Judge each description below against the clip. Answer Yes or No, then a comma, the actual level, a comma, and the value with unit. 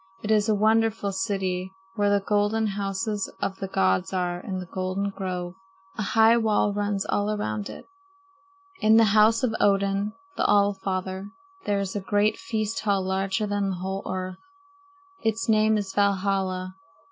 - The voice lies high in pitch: Yes, high, 200 Hz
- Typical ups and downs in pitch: No, narrow, 2.0 semitones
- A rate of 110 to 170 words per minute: Yes, average, 165 wpm